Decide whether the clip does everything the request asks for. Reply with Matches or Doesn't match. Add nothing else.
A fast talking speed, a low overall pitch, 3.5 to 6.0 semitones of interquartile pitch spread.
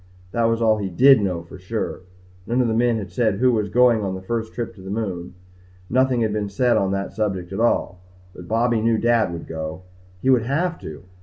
Matches